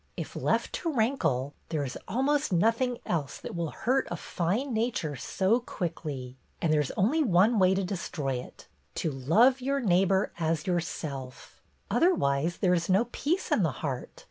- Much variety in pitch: Yes, wide, 7.6 semitones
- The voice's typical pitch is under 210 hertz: Yes, medium, 185 Hz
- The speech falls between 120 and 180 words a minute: Yes, average, 175 wpm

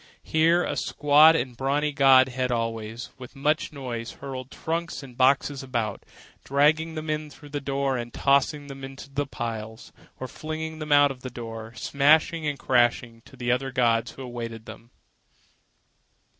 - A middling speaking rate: Yes, average, 160 wpm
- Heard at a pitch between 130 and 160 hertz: Yes, low, 135 Hz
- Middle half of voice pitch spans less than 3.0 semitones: No, average, 3.4 semitones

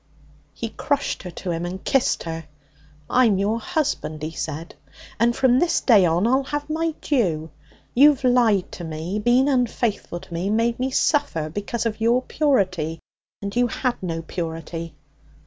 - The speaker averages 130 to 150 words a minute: No, average, 165 wpm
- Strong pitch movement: Yes, wide, 7.2 semitones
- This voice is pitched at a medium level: No, high, 220 Hz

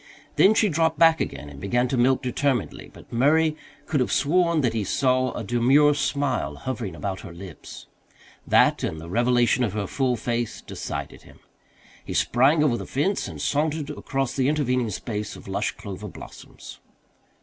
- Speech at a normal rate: Yes, average, 170 wpm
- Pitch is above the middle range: No, low, 130 Hz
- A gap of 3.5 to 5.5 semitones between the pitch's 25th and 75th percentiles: Yes, average, 4.3 semitones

